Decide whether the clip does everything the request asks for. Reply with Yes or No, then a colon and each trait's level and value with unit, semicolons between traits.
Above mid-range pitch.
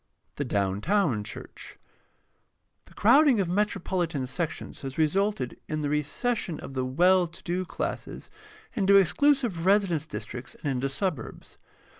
No: medium, 170 Hz